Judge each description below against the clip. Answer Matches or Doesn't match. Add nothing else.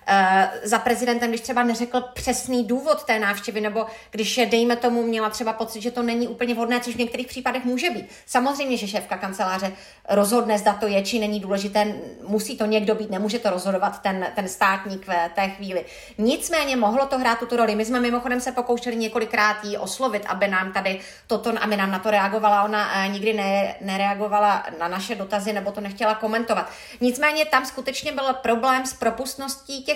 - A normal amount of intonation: Matches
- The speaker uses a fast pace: Matches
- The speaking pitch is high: Matches